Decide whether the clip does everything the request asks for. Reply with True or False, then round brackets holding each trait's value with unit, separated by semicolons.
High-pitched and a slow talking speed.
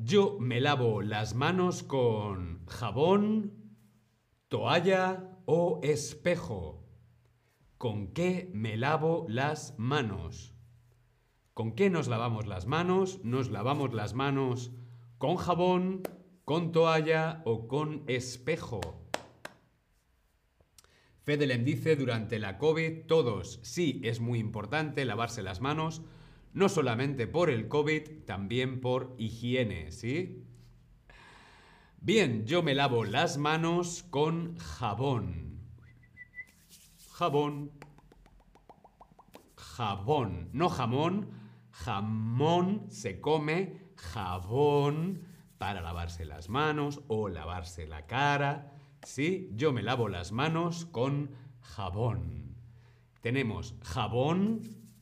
False (130 Hz; 95 wpm)